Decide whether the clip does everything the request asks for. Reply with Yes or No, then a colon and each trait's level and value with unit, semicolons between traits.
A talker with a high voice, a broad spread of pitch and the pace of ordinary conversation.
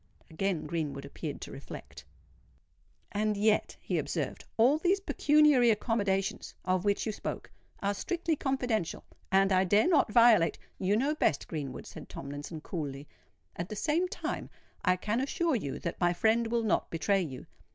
Yes: high, 205 Hz; wide, 6.0 semitones; average, 160 wpm